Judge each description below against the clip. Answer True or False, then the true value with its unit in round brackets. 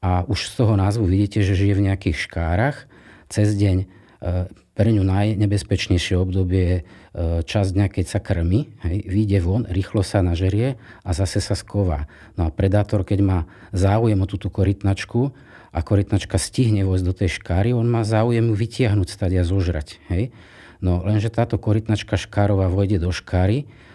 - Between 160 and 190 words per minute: True (165 wpm)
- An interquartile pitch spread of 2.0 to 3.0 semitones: True (2.5 semitones)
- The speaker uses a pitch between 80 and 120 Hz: True (100 Hz)